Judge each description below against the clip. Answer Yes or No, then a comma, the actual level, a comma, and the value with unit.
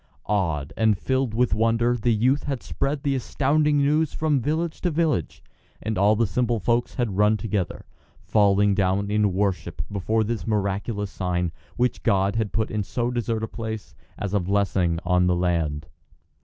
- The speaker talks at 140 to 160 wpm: No, average, 170 wpm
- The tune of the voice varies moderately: Yes, average, 3.9 semitones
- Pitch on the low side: Yes, low, 110 Hz